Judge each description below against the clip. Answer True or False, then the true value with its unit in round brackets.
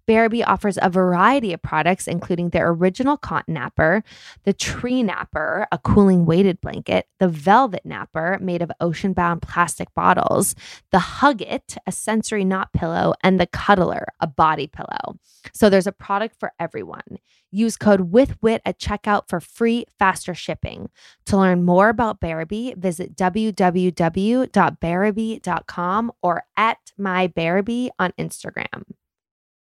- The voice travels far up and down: False (3.6 semitones)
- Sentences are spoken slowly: True (130 wpm)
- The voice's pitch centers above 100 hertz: True (190 Hz)